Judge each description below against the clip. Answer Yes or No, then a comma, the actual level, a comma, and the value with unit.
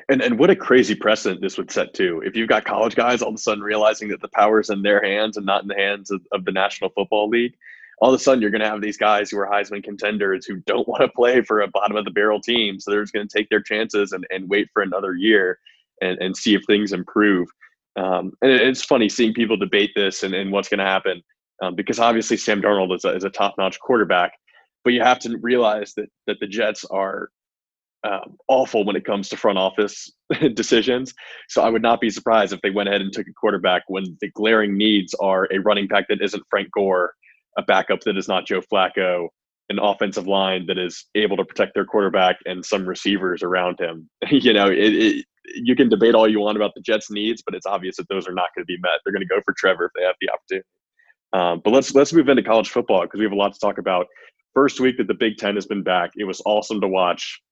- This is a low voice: Yes, low, 105 Hz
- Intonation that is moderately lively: No, narrow, 2.3 semitones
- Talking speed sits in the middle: No, fast, 255 wpm